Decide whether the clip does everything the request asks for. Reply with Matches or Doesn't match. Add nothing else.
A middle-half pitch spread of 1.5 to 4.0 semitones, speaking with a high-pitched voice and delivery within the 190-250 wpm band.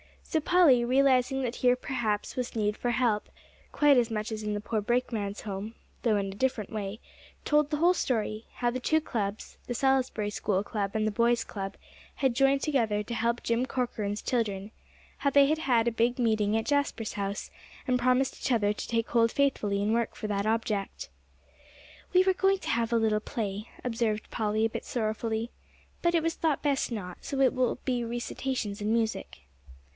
Matches